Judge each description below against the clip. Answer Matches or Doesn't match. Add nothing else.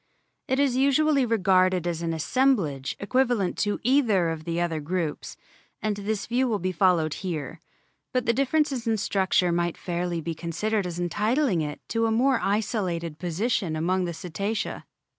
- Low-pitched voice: Doesn't match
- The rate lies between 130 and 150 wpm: Doesn't match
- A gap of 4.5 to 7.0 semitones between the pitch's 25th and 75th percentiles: Matches